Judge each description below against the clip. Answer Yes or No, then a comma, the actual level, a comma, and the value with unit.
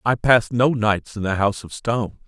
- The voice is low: Yes, low, 110 Hz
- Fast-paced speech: Yes, fast, 240 wpm